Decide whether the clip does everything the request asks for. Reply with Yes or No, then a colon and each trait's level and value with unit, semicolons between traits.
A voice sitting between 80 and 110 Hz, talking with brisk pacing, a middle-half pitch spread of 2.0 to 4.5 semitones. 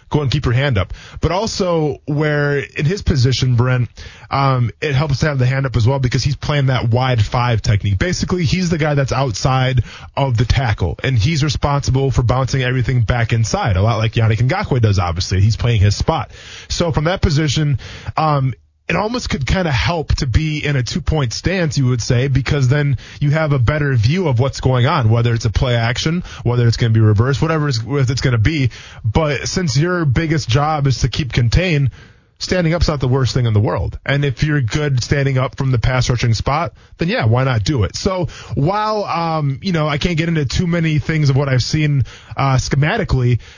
No: low, 130 Hz; fast, 220 wpm; average, 4.0 semitones